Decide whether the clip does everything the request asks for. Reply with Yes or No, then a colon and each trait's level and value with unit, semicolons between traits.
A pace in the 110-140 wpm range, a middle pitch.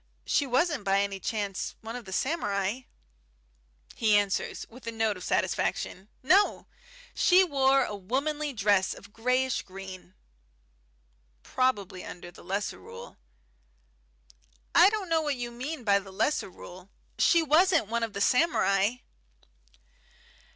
No: slow, 135 wpm; high, 225 Hz